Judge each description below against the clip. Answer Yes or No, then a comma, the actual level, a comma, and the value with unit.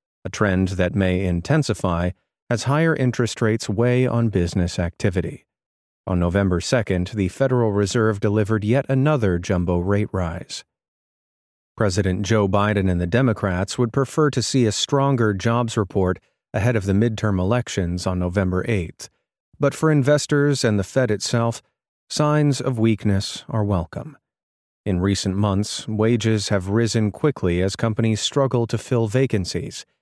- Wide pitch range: No, average, 4.4 semitones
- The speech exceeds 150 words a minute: No, average, 145 wpm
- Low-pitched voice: Yes, low, 105 Hz